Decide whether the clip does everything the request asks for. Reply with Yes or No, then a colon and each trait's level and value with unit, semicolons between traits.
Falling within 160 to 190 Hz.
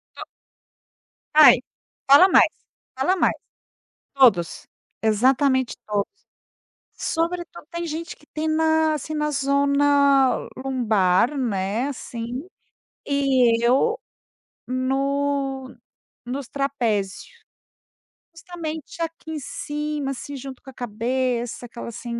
No: very high, 275 Hz